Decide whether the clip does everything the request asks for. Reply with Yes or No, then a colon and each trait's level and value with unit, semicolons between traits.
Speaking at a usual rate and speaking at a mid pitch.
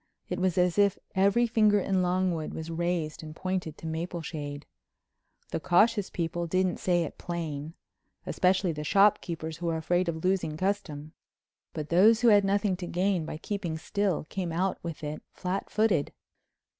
Yes: average, 155 wpm; medium, 175 Hz